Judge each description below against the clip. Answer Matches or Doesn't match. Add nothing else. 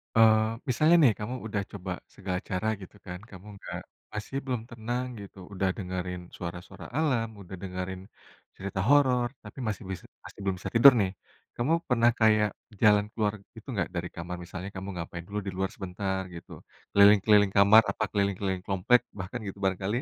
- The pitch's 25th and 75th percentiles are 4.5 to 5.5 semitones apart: Doesn't match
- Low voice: Matches